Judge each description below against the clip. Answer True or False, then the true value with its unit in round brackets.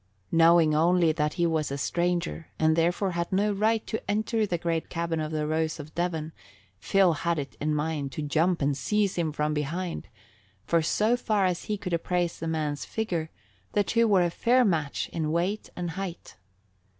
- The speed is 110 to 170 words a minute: False (190 wpm)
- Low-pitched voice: False (170 Hz)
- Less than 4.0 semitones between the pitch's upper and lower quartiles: True (3.1 semitones)